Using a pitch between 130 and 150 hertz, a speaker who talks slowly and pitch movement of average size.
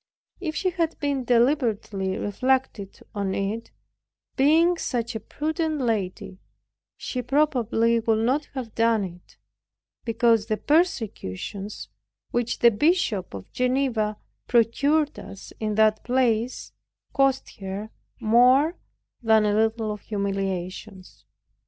No: high, 230 Hz; slow, 110 wpm; average, 4.3 semitones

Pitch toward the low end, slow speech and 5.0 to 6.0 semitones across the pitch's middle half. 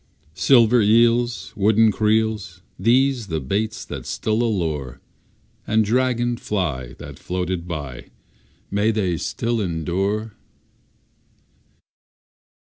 No: low, 105 Hz; slow, 95 wpm; average, 4.5 semitones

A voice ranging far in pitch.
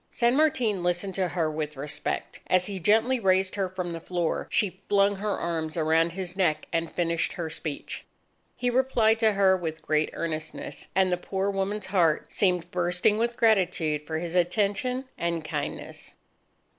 No: average, 3.5 semitones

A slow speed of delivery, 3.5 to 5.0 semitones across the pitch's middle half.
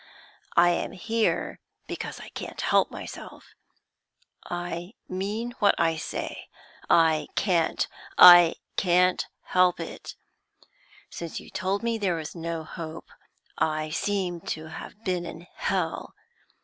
No: slow, 125 wpm; narrow, 2.6 semitones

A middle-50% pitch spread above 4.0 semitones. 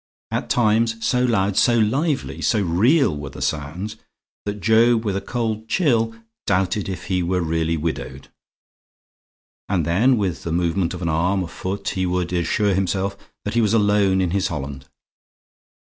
Yes: average, 4.4 semitones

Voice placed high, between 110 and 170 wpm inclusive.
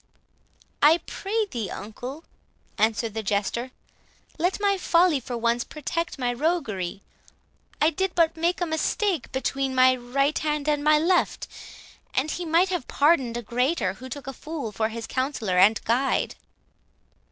Yes: very high, 275 Hz; average, 150 wpm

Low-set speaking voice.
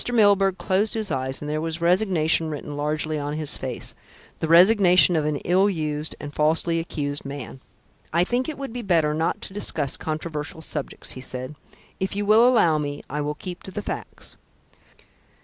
No: medium, 160 Hz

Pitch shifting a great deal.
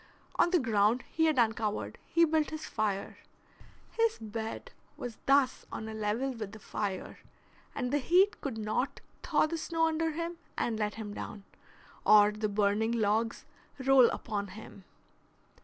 Yes: wide, 6.3 semitones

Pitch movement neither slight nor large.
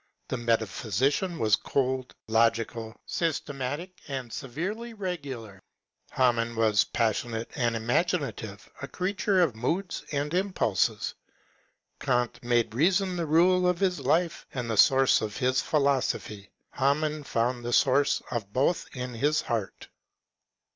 No: wide, 6.1 semitones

